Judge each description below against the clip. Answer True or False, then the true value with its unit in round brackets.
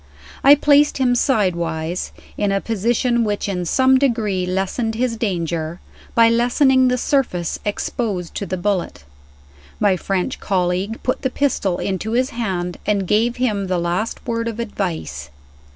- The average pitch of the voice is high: True (210 Hz)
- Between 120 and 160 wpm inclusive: True (150 wpm)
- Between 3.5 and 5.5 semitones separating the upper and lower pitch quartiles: True (4.9 semitones)